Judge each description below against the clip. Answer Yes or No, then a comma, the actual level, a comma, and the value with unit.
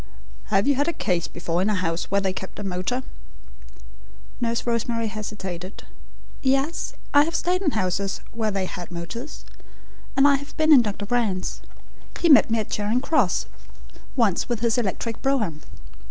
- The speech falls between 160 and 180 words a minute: Yes, average, 170 wpm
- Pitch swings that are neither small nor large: No, wide, 5.9 semitones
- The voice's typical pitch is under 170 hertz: No, high, 220 Hz